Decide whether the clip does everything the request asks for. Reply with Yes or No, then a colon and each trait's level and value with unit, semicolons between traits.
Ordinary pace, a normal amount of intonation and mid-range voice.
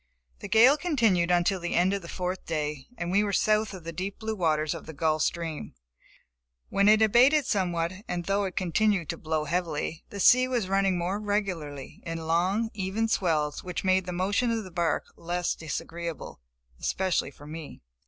Yes: average, 190 wpm; average, 3.6 semitones; medium, 180 Hz